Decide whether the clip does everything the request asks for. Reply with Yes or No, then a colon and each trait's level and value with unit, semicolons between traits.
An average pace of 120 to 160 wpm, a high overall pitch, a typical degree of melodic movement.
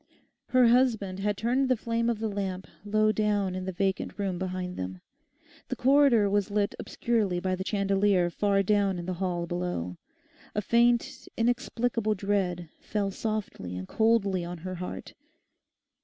Yes: average, 155 wpm; high, 200 Hz; average, 3.2 semitones